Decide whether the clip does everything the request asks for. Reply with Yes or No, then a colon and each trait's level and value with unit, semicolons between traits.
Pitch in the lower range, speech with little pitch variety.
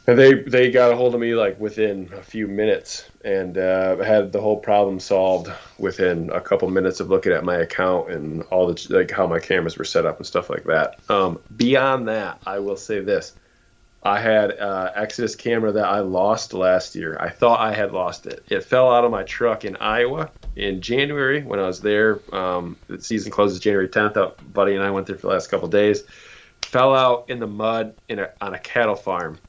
No: low, 105 Hz; average, 4.1 semitones